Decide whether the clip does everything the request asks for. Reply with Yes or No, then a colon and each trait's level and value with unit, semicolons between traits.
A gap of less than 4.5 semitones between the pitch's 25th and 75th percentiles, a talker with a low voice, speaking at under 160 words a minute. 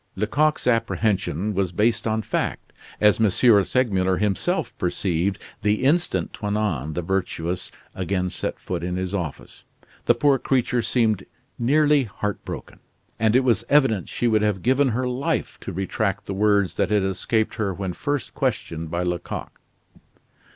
Yes: average, 4.1 semitones; low, 105 Hz; average, 150 wpm